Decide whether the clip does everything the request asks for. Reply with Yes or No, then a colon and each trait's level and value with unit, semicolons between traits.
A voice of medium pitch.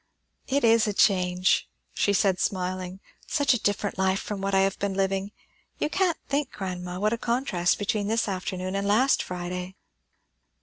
No: high, 195 Hz